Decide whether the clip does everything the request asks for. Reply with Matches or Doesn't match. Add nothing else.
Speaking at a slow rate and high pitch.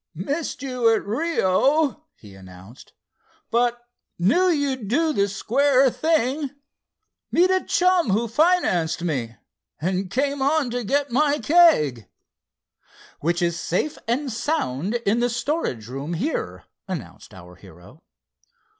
Matches